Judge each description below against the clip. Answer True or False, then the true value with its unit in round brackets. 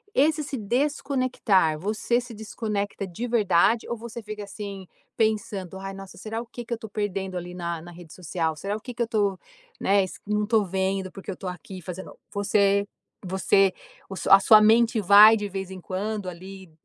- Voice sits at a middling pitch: False (200 Hz)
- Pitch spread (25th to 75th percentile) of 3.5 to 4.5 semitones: False (2.7 semitones)